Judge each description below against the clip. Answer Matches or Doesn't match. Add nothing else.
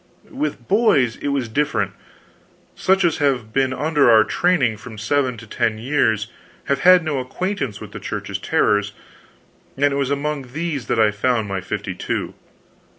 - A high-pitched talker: Doesn't match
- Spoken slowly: Doesn't match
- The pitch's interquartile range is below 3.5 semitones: Doesn't match